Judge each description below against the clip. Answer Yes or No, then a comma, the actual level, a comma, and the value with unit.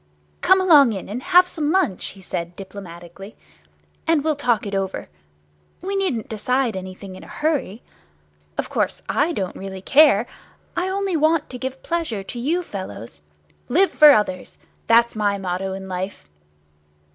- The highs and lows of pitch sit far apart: Yes, wide, 8.5 semitones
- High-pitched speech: Yes, high, 230 Hz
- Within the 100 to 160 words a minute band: Yes, average, 155 wpm